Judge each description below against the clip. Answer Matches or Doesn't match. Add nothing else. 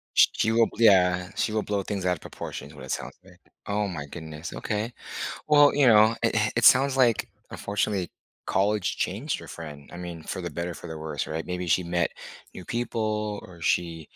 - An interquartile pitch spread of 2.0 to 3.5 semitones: Doesn't match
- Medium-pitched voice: Doesn't match